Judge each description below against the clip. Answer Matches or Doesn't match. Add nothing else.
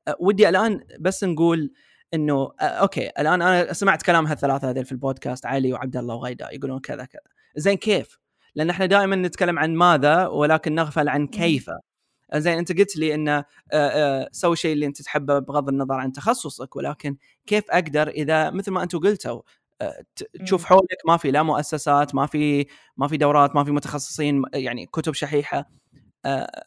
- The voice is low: Doesn't match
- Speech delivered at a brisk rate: Matches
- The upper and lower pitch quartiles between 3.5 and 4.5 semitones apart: Matches